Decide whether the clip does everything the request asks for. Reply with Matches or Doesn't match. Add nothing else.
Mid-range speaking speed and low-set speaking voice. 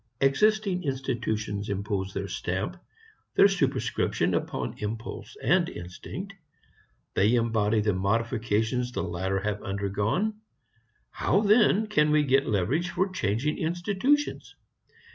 Doesn't match